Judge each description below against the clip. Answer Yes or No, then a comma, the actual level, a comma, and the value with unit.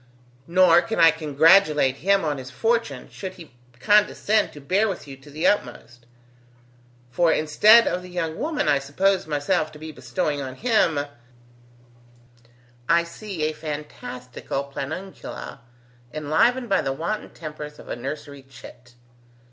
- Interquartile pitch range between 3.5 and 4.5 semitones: No, average, 5.0 semitones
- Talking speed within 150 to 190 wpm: No, average, 140 wpm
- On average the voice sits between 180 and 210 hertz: No, medium, 155 Hz